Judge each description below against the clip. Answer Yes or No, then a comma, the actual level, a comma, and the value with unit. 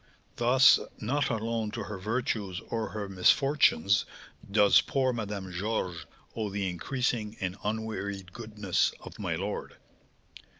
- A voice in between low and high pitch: No, low, 105 Hz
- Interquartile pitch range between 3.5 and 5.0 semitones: No, average, 3.1 semitones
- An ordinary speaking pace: No, slow, 125 wpm